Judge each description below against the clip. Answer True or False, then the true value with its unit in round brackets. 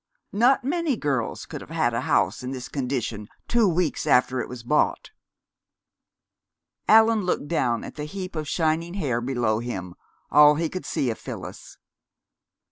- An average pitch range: False (6.9 semitones)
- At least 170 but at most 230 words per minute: False (160 wpm)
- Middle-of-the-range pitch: True (150 Hz)